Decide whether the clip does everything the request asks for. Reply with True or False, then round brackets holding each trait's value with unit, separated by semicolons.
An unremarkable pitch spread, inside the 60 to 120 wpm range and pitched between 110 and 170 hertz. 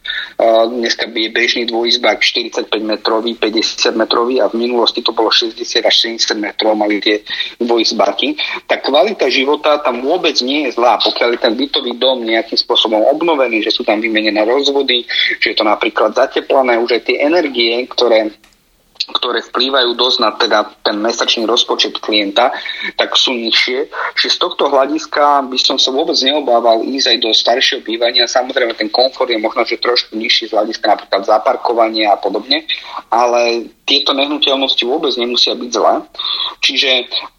False (3.3 semitones; 160 wpm; 120 Hz)